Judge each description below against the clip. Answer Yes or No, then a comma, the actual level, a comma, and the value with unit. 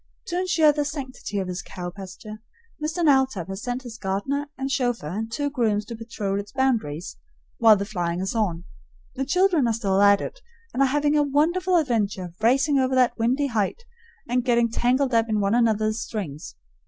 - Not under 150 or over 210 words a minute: Yes, average, 190 wpm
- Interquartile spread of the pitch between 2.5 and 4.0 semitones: No, average, 5.3 semitones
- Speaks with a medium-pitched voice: No, high, 235 Hz